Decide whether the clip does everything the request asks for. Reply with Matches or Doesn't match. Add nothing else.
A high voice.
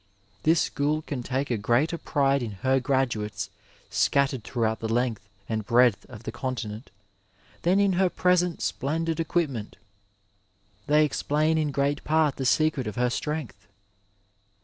Doesn't match